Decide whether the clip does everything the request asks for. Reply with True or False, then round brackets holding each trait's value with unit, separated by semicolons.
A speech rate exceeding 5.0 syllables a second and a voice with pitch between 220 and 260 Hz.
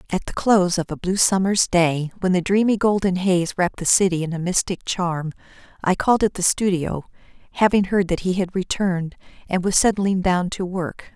False (5.3 syllables/s; 185 Hz)